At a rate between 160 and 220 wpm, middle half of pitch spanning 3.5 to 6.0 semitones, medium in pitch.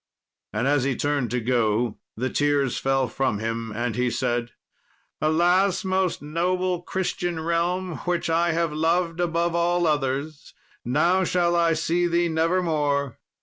No: average, 150 wpm; average, 4.6 semitones; medium, 160 Hz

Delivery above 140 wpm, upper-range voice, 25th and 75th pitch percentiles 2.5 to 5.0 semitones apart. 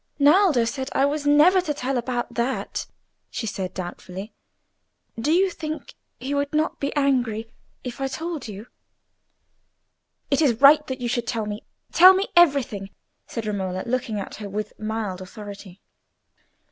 No: average, 155 wpm; very high, 250 Hz; wide, 5.4 semitones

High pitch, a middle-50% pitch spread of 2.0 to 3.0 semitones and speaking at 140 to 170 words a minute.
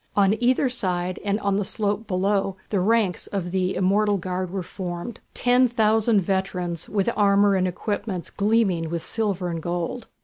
Yes: high, 195 Hz; average, 2.7 semitones; average, 165 wpm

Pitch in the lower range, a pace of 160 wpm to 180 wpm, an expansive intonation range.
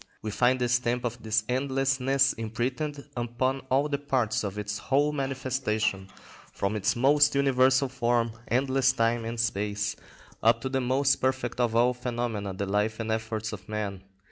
No: low, 120 Hz; average, 165 wpm; average, 3.3 semitones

